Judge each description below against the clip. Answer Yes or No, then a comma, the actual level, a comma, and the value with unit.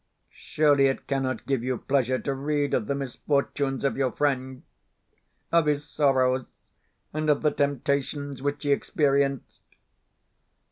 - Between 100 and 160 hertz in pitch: Yes, medium, 140 Hz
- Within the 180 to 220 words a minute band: No, slow, 135 wpm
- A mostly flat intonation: Yes, narrow, 1.4 semitones